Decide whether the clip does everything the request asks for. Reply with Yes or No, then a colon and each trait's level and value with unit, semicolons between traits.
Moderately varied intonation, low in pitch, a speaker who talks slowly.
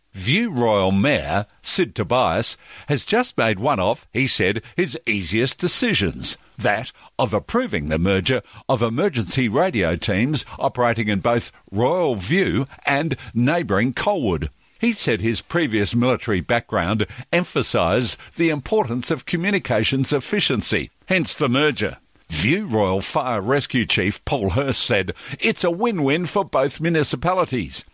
No: wide, 6.7 semitones; low, 130 Hz; slow, 130 wpm